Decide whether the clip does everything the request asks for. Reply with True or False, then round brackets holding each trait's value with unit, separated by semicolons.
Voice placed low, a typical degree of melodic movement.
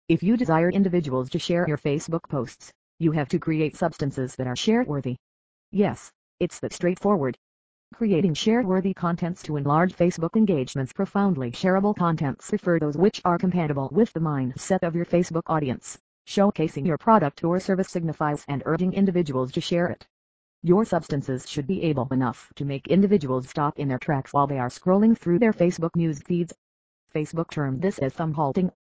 False (165 Hz; 4.7 semitones)